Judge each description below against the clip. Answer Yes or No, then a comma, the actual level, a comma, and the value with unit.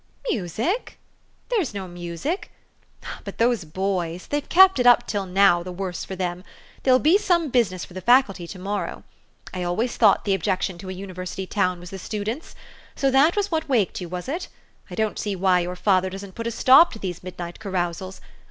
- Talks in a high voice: Yes, high, 195 Hz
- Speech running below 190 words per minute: No, average, 200 wpm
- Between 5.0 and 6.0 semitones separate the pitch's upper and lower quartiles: Yes, wide, 5.4 semitones